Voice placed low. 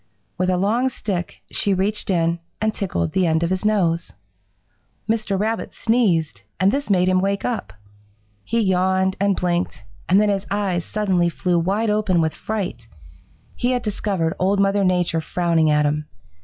No: high, 190 Hz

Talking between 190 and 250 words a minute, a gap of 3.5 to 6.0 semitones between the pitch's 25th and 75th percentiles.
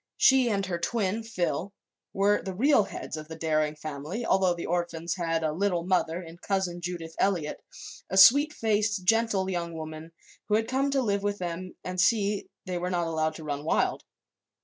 Yes: average, 195 wpm; average, 3.8 semitones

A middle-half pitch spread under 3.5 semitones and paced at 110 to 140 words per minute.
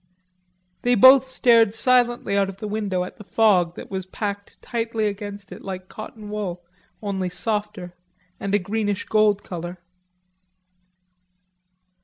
Yes: narrow, 2.6 semitones; slow, 135 wpm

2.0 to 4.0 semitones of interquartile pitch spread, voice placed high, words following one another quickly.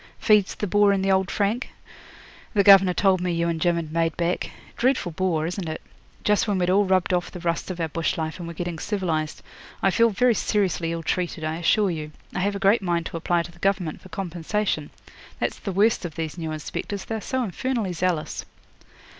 No: average, 3.1 semitones; medium, 180 Hz; fast, 220 wpm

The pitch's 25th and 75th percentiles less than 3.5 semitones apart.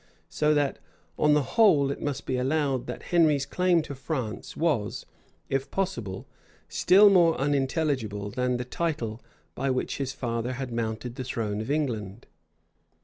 No: average, 4.3 semitones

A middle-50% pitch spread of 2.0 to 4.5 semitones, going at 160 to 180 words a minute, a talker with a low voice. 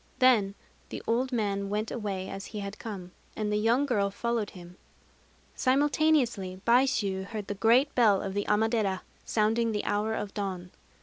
No: average, 3.0 semitones; average, 165 wpm; high, 210 Hz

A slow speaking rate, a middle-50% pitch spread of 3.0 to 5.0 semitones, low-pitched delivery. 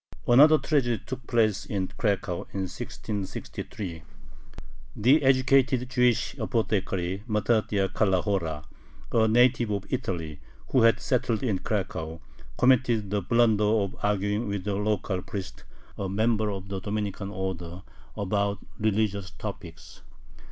Yes: slow, 120 wpm; average, 3.3 semitones; low, 105 Hz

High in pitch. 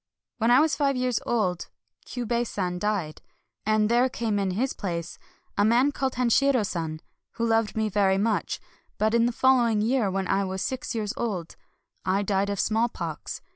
Yes: high, 215 Hz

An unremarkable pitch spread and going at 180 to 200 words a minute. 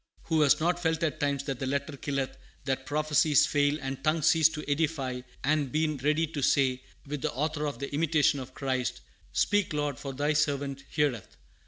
No: narrow, 2.2 semitones; average, 190 wpm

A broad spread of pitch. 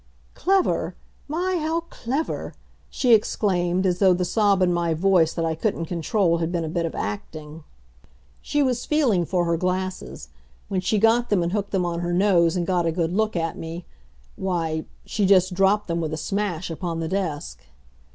No: average, 3.6 semitones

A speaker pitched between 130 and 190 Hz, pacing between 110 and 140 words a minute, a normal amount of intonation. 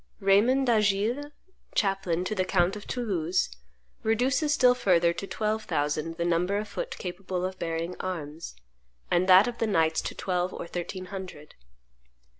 No: medium, 185 Hz; average, 155 wpm; average, 3.9 semitones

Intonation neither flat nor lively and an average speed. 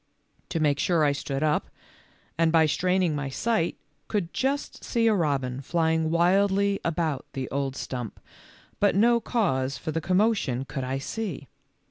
No: wide, 6.1 semitones; average, 160 wpm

